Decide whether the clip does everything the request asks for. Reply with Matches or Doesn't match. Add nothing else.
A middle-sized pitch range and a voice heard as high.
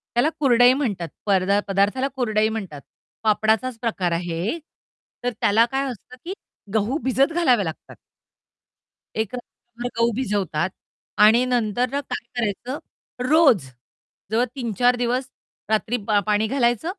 Matches